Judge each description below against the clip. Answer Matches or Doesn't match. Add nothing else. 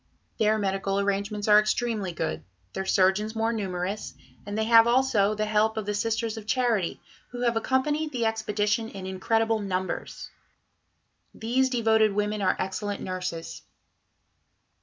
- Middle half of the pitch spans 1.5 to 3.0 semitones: Matches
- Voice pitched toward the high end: Matches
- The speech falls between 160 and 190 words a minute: Doesn't match